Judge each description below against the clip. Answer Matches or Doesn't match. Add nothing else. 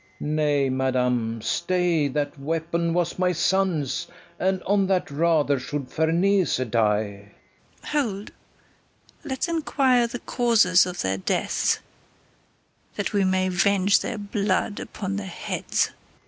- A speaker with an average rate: Doesn't match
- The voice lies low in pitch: Doesn't match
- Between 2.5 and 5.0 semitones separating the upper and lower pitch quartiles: Doesn't match